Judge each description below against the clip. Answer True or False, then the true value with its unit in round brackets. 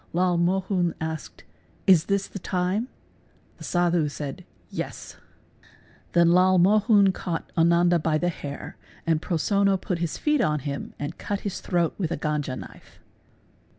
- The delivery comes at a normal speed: True (165 wpm)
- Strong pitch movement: False (3.1 semitones)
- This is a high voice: False (175 Hz)